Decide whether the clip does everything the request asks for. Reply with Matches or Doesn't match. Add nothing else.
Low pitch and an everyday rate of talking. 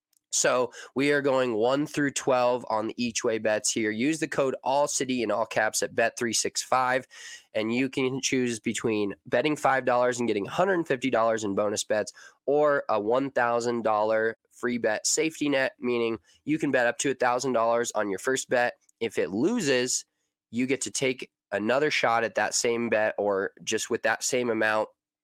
Matches